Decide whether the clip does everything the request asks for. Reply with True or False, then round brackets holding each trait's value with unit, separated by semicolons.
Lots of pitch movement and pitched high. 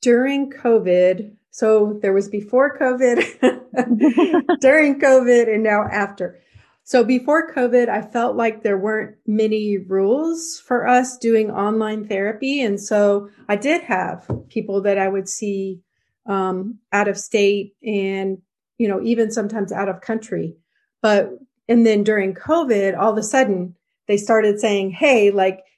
False (3.8 semitones; 215 Hz)